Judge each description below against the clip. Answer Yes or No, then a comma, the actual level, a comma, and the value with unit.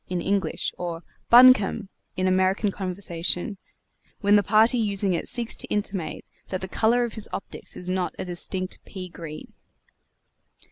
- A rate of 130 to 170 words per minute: Yes, average, 150 wpm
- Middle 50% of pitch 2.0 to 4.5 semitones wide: Yes, narrow, 2.5 semitones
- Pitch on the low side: No, high, 190 Hz